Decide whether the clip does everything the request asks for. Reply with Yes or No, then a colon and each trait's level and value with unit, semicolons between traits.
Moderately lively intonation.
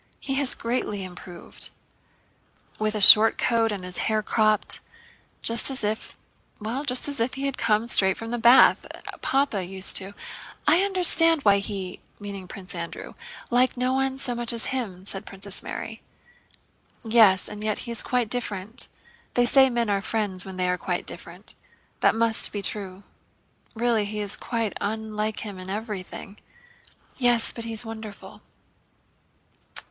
Yes: average, 3.4 semitones